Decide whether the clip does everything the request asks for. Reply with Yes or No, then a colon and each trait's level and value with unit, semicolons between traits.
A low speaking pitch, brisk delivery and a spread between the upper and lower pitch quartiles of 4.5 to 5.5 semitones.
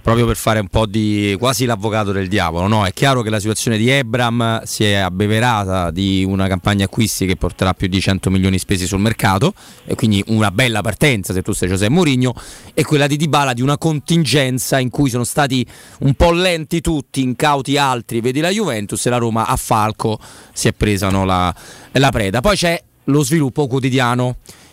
Yes: low, 115 Hz; fast, 200 wpm; average, 4.9 semitones